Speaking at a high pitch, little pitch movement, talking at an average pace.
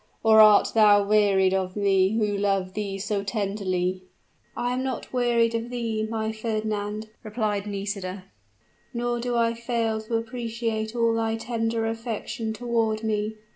Yes: high, 220 Hz; narrow, 2.1 semitones; average, 145 wpm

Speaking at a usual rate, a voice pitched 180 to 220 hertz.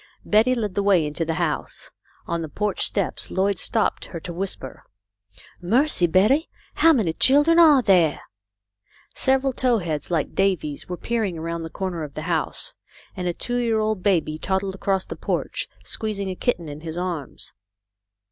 Yes: average, 175 wpm; medium, 185 Hz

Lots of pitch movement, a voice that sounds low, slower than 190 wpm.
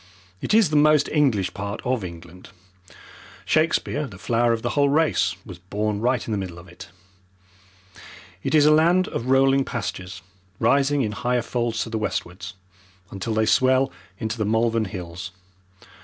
Yes: wide, 5.7 semitones; low, 115 Hz; average, 165 wpm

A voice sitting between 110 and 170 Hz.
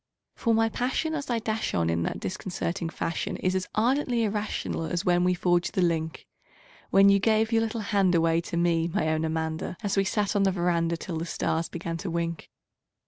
No: medium, 180 Hz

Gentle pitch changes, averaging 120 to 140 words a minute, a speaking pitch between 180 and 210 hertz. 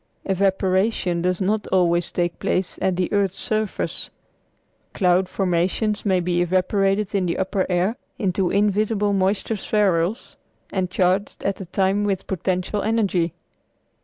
Yes: narrow, 2.0 semitones; slow, 135 wpm; high, 190 Hz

